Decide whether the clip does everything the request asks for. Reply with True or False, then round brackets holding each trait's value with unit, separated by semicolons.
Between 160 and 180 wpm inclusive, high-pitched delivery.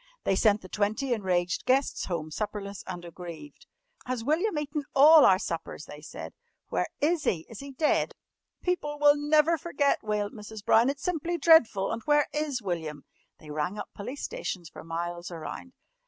True (170 wpm; 220 Hz)